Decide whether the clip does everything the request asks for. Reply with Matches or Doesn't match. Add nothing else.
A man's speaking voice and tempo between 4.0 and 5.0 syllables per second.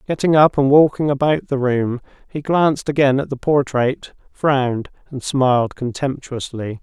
Matches